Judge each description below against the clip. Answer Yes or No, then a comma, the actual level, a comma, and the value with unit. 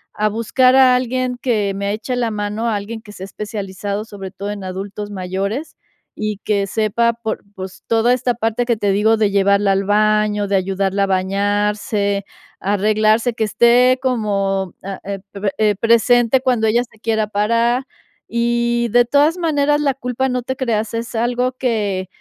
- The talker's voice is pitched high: Yes, high, 215 Hz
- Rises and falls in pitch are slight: No, average, 3.1 semitones